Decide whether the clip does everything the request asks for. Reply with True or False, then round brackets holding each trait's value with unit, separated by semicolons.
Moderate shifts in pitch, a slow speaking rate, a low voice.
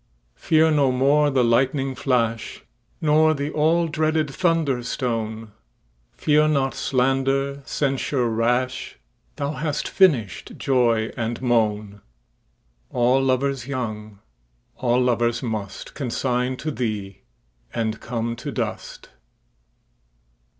True (3.9 semitones; 90 wpm; 125 Hz)